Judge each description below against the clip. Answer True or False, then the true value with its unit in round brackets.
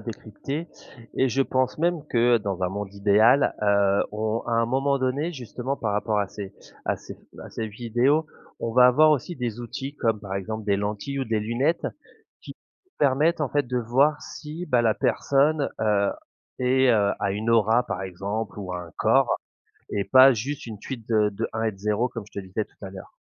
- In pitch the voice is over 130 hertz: False (115 Hz)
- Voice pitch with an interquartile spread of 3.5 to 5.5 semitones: True (4.5 semitones)